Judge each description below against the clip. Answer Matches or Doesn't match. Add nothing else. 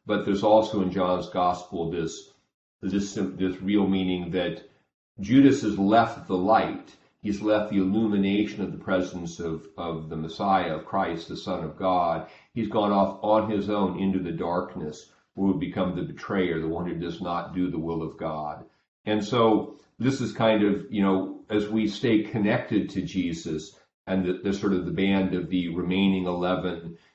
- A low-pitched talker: Matches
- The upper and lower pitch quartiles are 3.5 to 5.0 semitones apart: Doesn't match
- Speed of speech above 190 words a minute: Doesn't match